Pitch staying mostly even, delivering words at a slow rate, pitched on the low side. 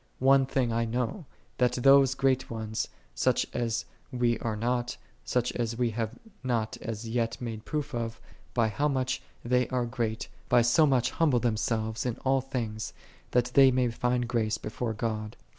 No: narrow, 2.1 semitones; average, 175 wpm; low, 120 Hz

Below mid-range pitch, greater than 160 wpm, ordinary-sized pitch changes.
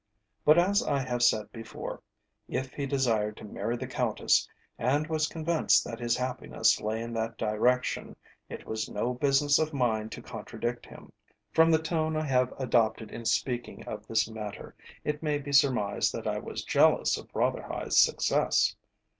Yes: low, 125 Hz; average, 170 wpm; average, 4.5 semitones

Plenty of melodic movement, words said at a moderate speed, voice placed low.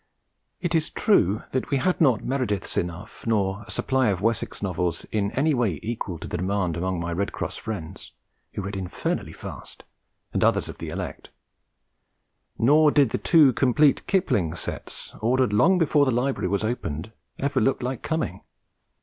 Yes: wide, 6.3 semitones; average, 170 wpm; low, 110 Hz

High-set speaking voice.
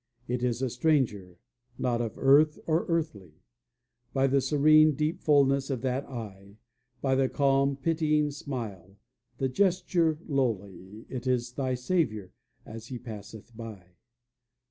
No: low, 130 Hz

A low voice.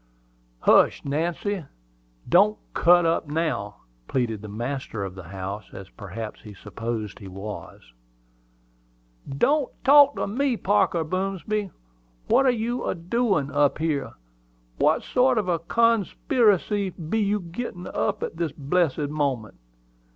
No: medium, 165 Hz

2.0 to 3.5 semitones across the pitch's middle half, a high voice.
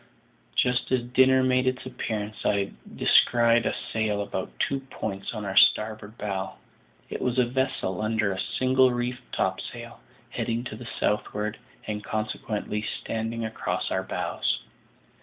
No: average, 2.9 semitones; low, 110 Hz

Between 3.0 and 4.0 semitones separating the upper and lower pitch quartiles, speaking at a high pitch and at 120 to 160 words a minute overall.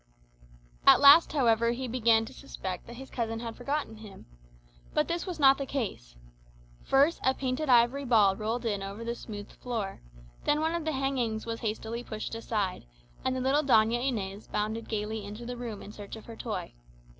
No: average, 3.6 semitones; high, 235 Hz; average, 190 wpm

